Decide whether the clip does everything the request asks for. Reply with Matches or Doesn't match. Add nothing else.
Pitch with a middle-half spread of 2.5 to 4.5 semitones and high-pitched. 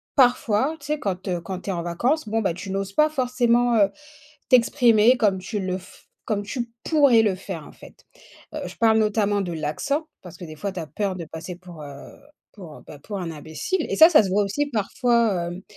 Doesn't match